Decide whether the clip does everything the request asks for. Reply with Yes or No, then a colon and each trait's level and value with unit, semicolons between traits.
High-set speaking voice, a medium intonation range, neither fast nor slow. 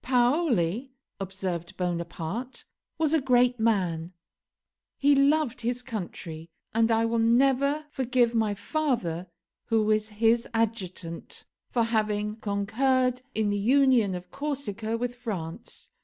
No: high, 225 Hz; average, 4.2 semitones; slow, 120 wpm